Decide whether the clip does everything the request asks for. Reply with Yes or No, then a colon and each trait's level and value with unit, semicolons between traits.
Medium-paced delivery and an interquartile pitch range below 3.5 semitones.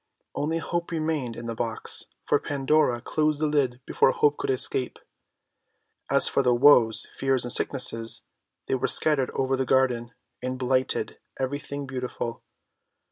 Yes: average, 150 wpm; average, 2.9 semitones